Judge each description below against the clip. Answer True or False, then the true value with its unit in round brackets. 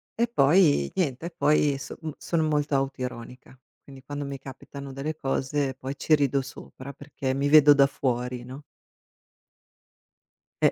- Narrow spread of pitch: True (1.9 semitones)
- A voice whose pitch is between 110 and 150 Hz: True (140 Hz)